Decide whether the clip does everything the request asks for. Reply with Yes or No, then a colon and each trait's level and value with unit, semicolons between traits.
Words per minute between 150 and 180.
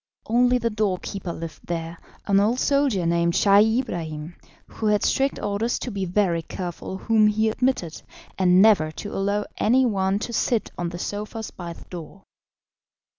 Yes: average, 170 wpm